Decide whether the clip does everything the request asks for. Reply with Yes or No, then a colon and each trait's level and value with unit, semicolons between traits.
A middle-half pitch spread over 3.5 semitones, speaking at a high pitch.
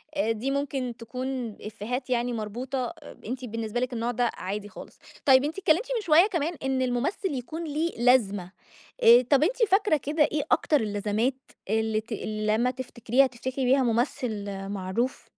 Yes: average, 4.0 semitones; very high, 250 Hz